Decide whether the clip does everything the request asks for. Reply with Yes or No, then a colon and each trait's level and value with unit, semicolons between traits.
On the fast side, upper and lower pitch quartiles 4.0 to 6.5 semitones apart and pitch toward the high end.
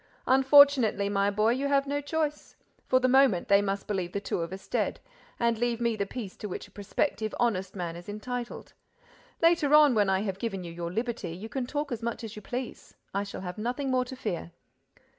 Yes: fast, 210 wpm; average, 4.7 semitones; high, 225 Hz